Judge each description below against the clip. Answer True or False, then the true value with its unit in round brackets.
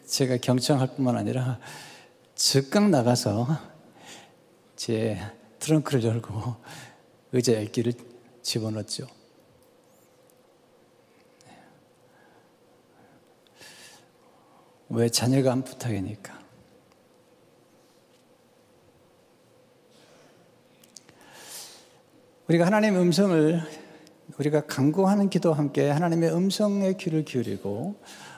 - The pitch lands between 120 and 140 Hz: True (135 Hz)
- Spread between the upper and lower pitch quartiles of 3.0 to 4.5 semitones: False (5.2 semitones)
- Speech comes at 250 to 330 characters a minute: False (160 characters per minute)